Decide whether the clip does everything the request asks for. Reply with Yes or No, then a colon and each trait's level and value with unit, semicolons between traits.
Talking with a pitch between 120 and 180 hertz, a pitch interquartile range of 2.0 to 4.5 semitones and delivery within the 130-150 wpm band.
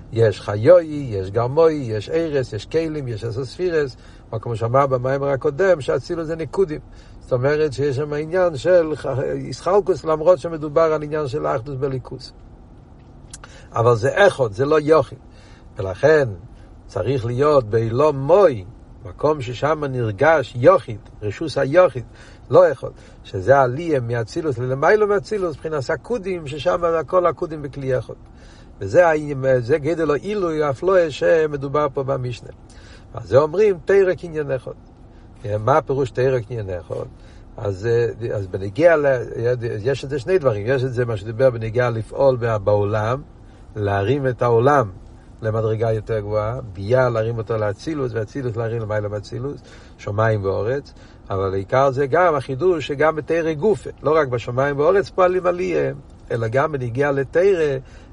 No: low, 135 Hz; wide, 5.6 semitones; average, 135 wpm